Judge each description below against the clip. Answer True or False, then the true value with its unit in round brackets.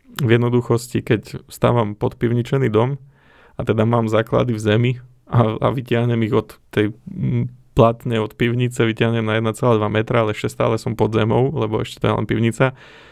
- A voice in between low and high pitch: False (115 Hz)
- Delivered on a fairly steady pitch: True (2.1 semitones)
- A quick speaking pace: True (170 wpm)